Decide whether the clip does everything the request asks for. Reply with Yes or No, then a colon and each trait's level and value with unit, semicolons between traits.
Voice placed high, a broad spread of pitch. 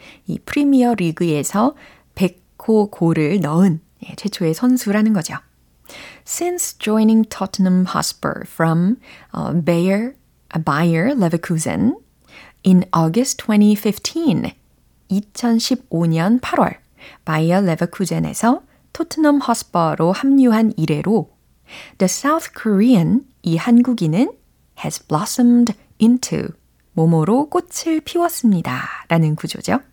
Yes: high, 210 Hz; wide, 6.4 semitones